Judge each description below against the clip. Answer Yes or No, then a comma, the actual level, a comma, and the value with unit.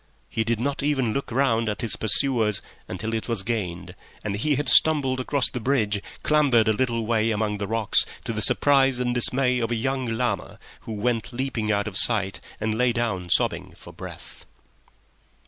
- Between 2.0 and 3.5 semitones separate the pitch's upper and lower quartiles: Yes, average, 3.2 semitones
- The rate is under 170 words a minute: No, average, 185 wpm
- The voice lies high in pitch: No, low, 115 Hz